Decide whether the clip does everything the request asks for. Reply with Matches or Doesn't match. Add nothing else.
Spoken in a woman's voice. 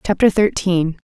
Matches